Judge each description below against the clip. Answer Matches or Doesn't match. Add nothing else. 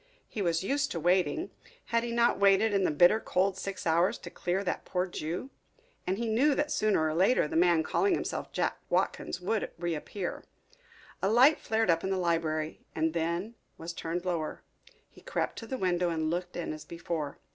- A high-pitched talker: Doesn't match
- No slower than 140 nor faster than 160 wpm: Doesn't match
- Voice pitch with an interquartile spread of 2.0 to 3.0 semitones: Doesn't match